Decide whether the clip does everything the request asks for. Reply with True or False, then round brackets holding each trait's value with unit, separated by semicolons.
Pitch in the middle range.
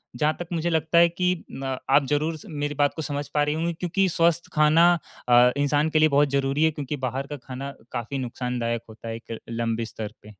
True (145 Hz)